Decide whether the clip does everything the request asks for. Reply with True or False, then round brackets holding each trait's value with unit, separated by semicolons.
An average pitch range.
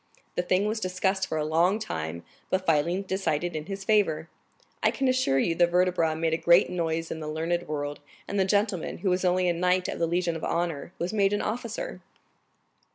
True (3.0 semitones)